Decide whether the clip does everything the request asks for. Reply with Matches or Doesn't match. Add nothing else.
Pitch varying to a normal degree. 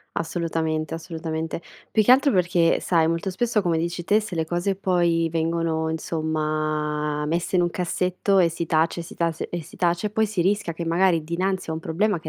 Doesn't match